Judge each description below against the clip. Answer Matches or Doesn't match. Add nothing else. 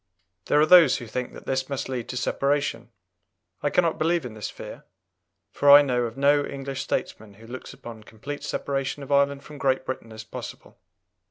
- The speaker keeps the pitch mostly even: Doesn't match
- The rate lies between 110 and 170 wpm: Doesn't match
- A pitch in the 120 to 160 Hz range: Matches